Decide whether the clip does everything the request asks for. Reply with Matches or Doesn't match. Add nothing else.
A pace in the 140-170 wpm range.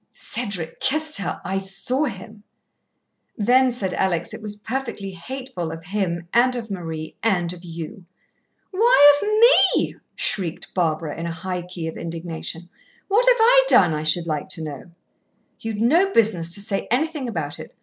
Matches